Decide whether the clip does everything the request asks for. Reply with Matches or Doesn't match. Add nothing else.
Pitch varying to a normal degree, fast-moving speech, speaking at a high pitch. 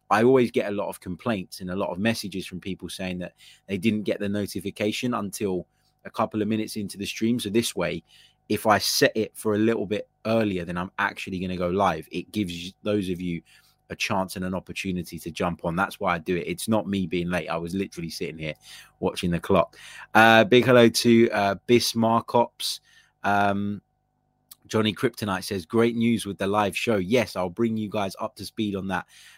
Doesn't match